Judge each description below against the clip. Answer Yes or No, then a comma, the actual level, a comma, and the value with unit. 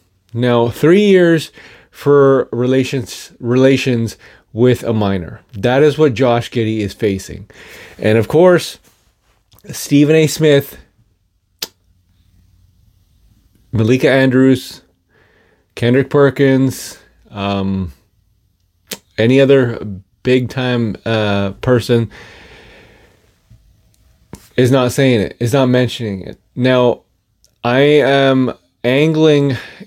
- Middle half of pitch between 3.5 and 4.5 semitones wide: No, average, 4.9 semitones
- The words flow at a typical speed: No, slow, 90 wpm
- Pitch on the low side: Yes, low, 120 Hz